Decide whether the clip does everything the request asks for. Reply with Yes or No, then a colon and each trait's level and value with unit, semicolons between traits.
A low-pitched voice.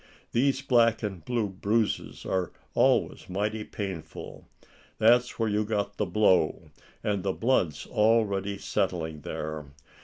Yes: low, 105 Hz